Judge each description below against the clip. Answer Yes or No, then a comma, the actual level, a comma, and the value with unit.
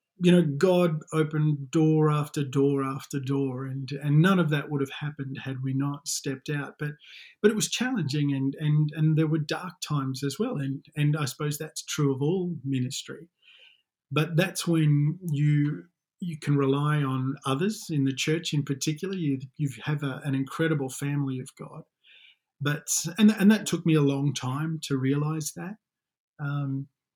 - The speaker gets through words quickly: No, average, 180 wpm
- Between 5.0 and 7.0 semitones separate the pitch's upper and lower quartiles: No, narrow, 2.5 semitones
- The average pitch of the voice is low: No, medium, 150 Hz